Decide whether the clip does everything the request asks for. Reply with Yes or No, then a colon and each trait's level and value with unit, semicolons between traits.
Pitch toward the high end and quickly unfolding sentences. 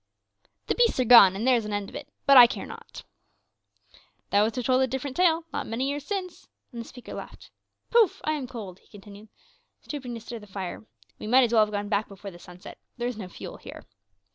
Yes: high, 235 Hz; fast, 240 wpm